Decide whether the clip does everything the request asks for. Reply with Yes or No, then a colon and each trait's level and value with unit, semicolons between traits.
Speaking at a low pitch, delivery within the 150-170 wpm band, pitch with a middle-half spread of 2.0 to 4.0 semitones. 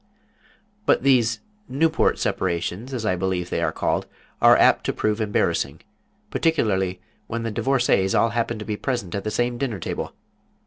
No: low, 110 Hz; average, 165 wpm; average, 4.5 semitones